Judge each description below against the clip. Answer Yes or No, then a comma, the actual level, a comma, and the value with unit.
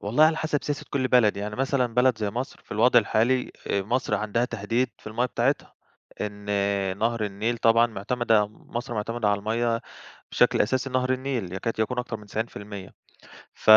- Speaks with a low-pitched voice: Yes, low, 115 Hz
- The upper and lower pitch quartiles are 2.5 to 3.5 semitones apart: Yes, average, 3.1 semitones